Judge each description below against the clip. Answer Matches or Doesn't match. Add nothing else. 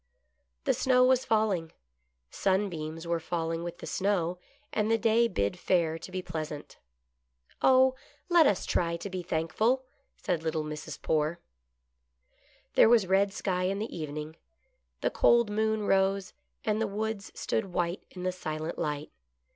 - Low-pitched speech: Doesn't match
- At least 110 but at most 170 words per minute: Matches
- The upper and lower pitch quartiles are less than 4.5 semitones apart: Doesn't match